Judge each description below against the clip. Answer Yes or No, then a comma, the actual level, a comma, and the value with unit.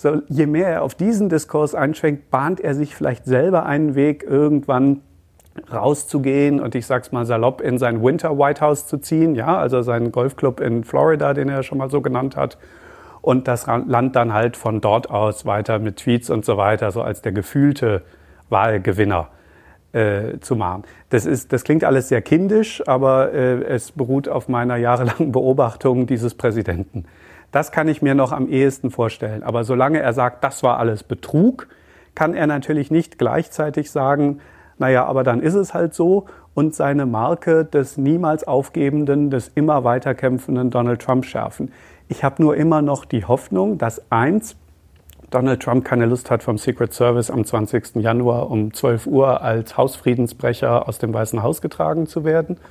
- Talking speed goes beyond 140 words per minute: Yes, average, 175 wpm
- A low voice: Yes, low, 130 Hz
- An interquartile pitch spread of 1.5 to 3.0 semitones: No, average, 3.7 semitones